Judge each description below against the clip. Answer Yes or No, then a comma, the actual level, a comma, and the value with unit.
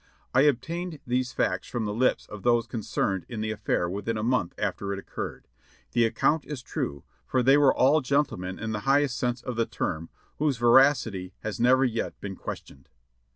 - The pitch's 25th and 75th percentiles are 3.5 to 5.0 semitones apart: Yes, average, 4.3 semitones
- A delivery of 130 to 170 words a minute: No, average, 195 wpm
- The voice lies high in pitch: No, low, 120 Hz